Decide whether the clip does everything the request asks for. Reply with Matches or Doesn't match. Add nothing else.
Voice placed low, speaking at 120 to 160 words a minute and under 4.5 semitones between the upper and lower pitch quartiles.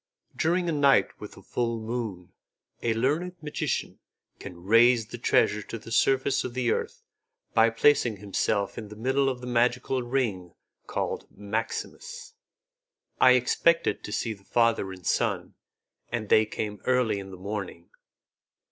Matches